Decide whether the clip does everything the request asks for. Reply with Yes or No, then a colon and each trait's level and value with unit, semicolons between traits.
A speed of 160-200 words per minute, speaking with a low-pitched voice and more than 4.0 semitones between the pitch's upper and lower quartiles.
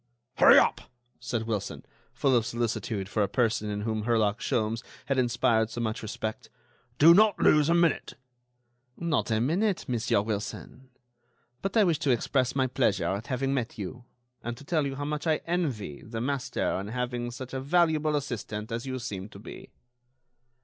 Yes: average, 175 wpm; low, 120 Hz; average, 4.5 semitones